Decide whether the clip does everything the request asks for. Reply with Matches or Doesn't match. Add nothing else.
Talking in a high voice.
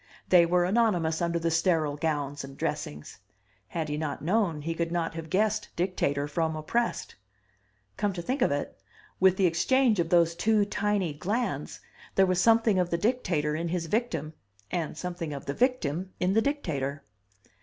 Doesn't match